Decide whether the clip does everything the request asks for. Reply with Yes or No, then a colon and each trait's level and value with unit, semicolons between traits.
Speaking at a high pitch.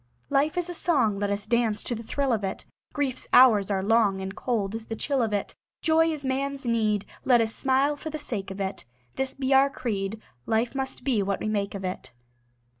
Yes: high, 230 Hz